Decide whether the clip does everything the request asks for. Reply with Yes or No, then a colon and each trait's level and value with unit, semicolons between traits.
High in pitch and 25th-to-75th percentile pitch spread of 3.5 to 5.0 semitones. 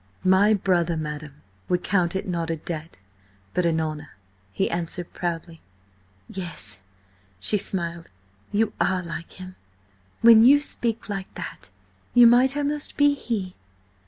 No: medium, 180 Hz; average, 4.6 semitones